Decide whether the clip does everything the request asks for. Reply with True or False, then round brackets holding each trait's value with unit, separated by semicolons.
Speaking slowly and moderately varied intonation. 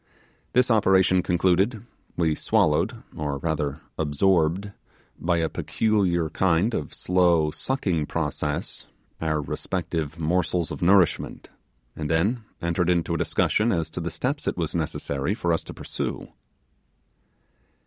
True (130 wpm; 3.1 semitones)